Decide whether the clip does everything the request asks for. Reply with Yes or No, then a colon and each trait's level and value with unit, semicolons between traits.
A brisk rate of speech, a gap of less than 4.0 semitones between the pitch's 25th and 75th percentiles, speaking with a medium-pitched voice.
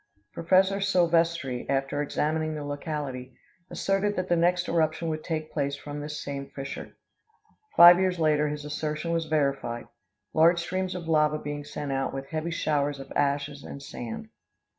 No: average, 160 wpm; average, 3.0 semitones; medium, 155 Hz